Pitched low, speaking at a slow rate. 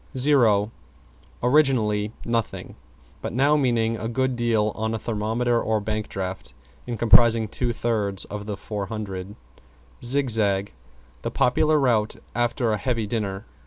Yes: low, 115 Hz; slow, 130 wpm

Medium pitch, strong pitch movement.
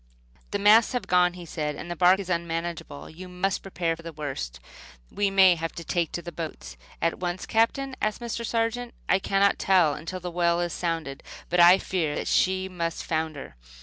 No: medium, 175 Hz; average, 2.7 semitones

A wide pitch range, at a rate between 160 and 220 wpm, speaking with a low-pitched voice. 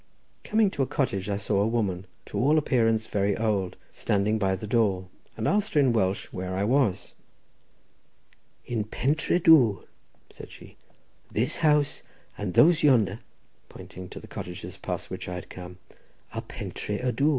Yes: wide, 5.9 semitones; average, 165 wpm; low, 110 Hz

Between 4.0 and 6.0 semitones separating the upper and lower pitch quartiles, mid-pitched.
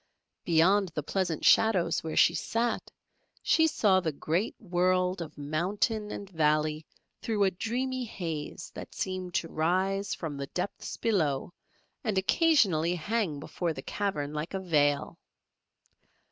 Yes: average, 4.5 semitones; medium, 180 Hz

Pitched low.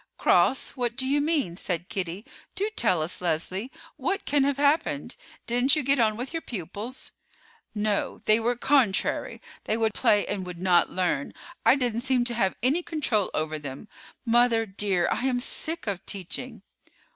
No: high, 230 Hz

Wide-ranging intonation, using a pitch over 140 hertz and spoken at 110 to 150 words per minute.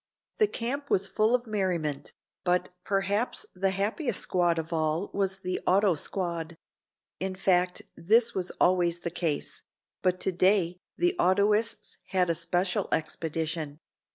No: average, 2.9 semitones; medium, 185 Hz; slow, 135 wpm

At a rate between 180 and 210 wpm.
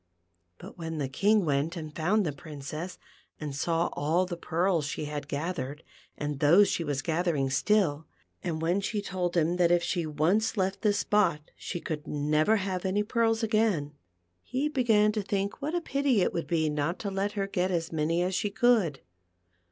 Yes: average, 190 wpm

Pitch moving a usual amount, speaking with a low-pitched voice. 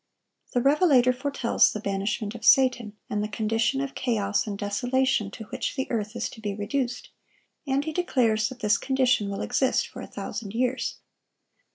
No: average, 3.9 semitones; high, 240 Hz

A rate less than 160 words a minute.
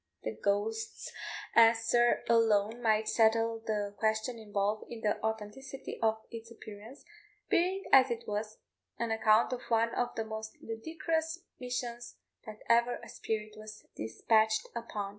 Yes: average, 140 wpm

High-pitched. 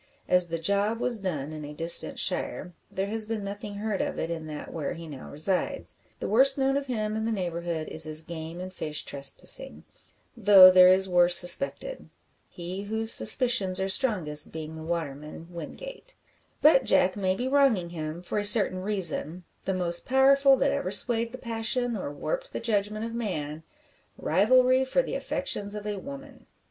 Yes: high, 195 Hz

